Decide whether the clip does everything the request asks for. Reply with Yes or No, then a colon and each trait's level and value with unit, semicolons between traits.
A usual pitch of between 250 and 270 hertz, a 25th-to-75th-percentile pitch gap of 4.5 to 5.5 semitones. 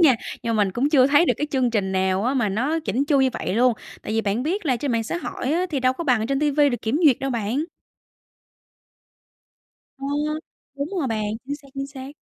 No: very high, 265 Hz; average, 4.1 semitones